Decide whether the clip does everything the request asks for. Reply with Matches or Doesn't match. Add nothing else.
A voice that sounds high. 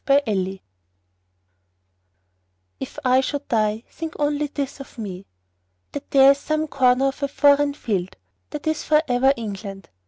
Matches